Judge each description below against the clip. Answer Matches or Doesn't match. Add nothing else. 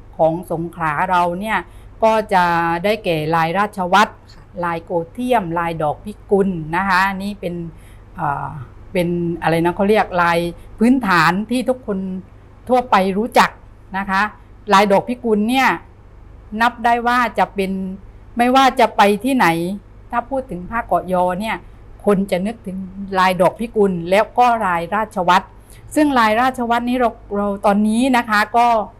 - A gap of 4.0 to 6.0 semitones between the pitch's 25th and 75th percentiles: Matches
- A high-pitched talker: Matches